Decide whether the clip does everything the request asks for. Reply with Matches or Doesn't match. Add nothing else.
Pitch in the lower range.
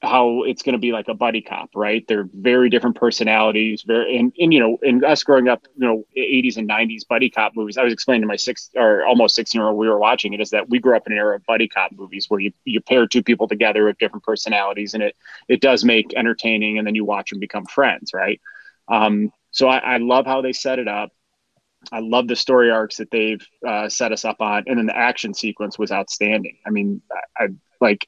Matches